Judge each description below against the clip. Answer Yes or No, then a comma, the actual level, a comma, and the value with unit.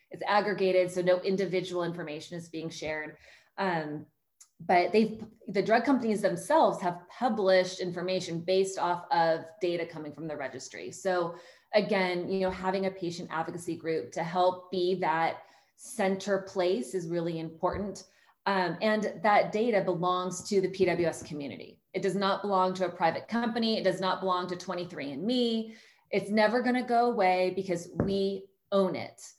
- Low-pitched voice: No, medium, 185 Hz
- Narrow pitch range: Yes, narrow, 2.3 semitones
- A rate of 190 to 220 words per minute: No, average, 160 wpm